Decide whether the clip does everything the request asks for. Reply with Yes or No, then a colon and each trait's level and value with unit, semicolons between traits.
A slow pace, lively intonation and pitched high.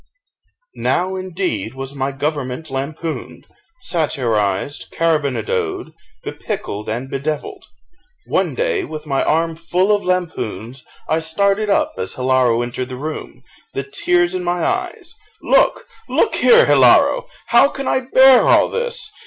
No: slow, 130 wpm; wide, 7.8 semitones; medium, 160 Hz